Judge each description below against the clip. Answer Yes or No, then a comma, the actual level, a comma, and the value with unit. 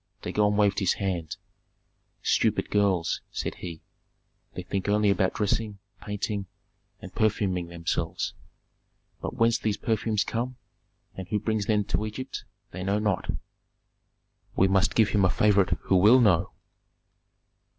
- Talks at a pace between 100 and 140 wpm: Yes, slow, 135 wpm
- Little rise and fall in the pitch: Yes, narrow, 2.2 semitones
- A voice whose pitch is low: Yes, low, 100 Hz